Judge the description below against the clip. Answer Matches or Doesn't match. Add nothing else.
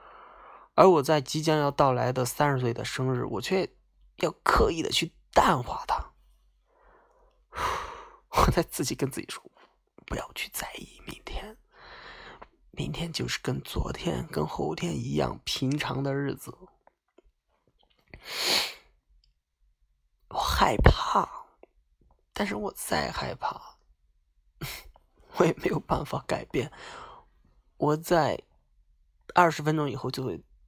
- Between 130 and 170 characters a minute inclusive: Matches